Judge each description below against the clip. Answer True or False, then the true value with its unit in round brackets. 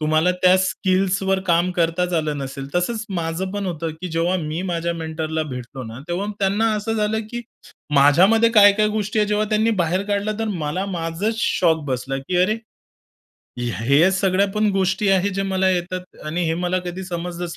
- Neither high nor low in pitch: True (180 Hz)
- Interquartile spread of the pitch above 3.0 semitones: True (3.5 semitones)